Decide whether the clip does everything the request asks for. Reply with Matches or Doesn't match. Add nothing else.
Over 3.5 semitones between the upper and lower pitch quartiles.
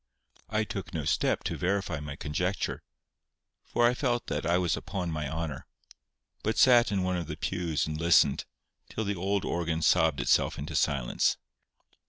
Matches